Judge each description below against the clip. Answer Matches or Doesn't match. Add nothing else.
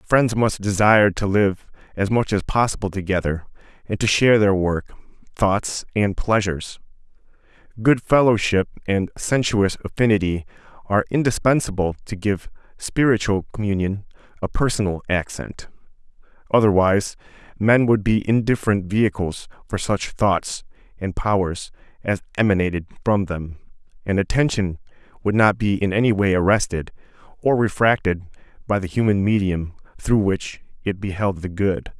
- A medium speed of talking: Doesn't match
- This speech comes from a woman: Doesn't match